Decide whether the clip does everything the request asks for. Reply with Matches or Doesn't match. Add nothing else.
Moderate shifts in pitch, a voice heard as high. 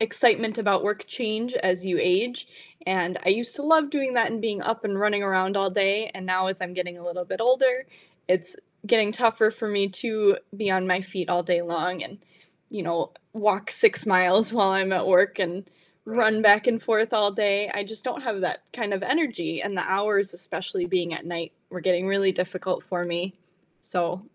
Matches